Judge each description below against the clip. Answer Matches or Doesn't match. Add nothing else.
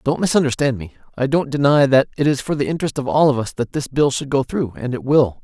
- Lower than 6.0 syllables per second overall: Doesn't match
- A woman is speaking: Doesn't match